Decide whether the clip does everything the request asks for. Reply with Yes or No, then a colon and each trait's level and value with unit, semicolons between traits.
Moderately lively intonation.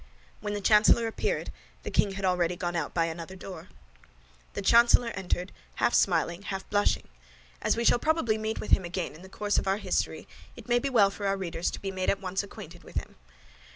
Yes: average, 3.1 semitones